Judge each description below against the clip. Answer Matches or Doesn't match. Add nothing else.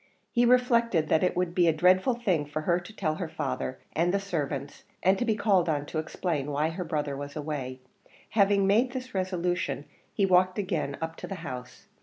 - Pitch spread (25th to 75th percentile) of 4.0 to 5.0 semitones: Matches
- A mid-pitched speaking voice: Matches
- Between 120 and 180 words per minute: Doesn't match